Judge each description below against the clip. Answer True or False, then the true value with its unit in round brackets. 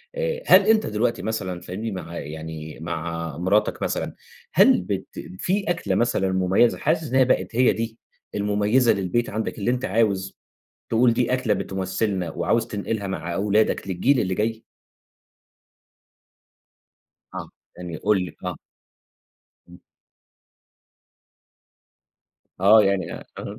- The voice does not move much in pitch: False (4.2 semitones)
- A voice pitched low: True (105 Hz)